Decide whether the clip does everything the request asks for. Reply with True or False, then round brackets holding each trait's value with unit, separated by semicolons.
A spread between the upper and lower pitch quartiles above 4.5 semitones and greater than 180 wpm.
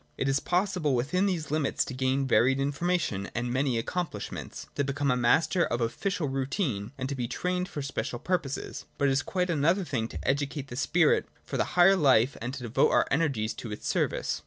True (5.0 semitones; 205 wpm)